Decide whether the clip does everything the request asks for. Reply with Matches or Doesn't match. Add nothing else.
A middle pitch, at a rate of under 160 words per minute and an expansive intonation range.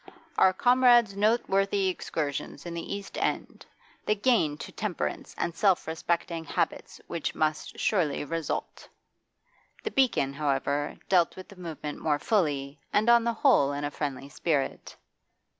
Matches